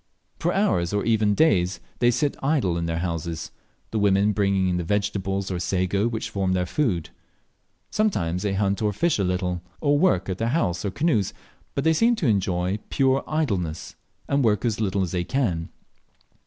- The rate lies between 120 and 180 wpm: No, average, 190 wpm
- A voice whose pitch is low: Yes, low, 100 Hz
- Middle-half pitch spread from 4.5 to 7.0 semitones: Yes, average, 5.3 semitones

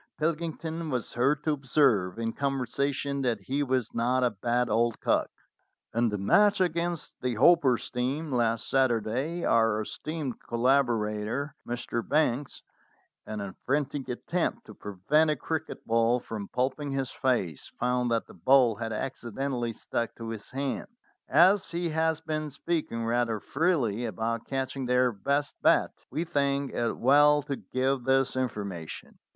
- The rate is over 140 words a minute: Yes, average, 150 wpm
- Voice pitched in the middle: No, low, 130 Hz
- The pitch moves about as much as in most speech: Yes, average, 4.1 semitones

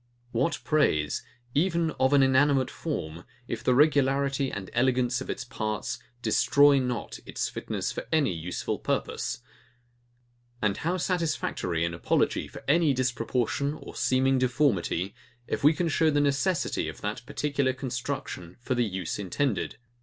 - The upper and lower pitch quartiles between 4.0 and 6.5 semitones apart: Yes, average, 4.6 semitones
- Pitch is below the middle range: Yes, low, 130 Hz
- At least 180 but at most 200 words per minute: No, average, 145 wpm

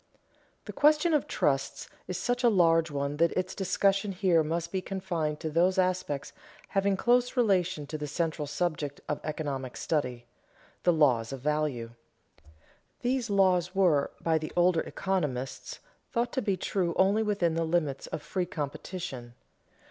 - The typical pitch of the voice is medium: Yes, medium, 170 Hz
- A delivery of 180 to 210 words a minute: No, average, 155 wpm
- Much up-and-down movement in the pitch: No, average, 4.5 semitones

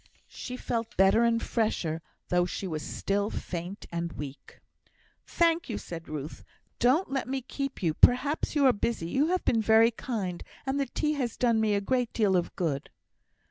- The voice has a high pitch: Yes, high, 225 Hz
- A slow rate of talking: No, average, 180 wpm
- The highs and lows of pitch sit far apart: Yes, wide, 6.5 semitones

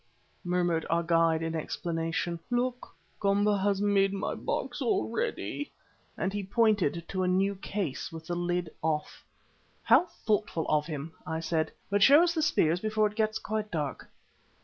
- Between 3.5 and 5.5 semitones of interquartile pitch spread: Yes, average, 4.4 semitones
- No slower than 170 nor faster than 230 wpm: No, average, 160 wpm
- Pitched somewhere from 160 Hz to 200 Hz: Yes, medium, 185 Hz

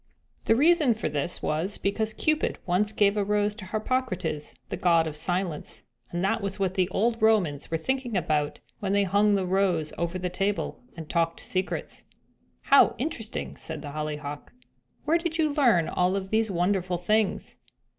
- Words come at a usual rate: Yes, average, 175 wpm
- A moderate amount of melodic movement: Yes, average, 4.3 semitones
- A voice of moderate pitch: No, high, 195 Hz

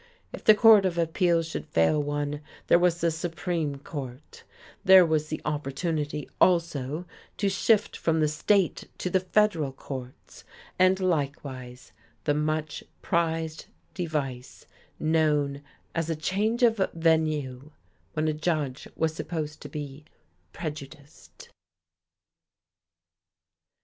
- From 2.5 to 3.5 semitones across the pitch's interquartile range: Yes, average, 2.8 semitones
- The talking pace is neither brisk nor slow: No, slow, 120 wpm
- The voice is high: No, medium, 155 Hz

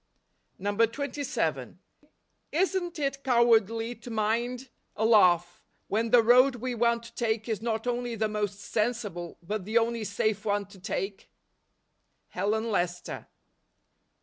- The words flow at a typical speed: No, slow, 125 wpm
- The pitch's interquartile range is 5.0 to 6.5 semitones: No, average, 2.7 semitones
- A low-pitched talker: No, high, 225 Hz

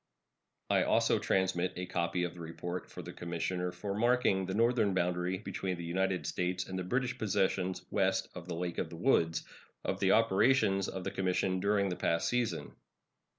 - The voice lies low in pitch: Yes, very low, 95 Hz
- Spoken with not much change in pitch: Yes, narrow, 2.0 semitones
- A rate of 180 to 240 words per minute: Yes, average, 185 wpm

